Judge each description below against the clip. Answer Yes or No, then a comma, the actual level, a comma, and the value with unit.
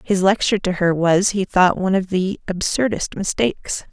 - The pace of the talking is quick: No, average, 185 wpm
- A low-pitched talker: No, high, 190 Hz